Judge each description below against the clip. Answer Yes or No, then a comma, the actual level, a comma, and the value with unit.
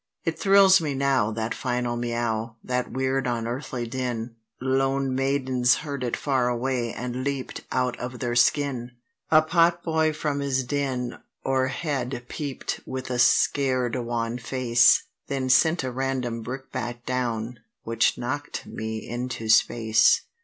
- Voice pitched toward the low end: Yes, low, 125 Hz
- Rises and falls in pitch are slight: Yes, narrow, 2.2 semitones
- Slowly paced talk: Yes, slow, 130 wpm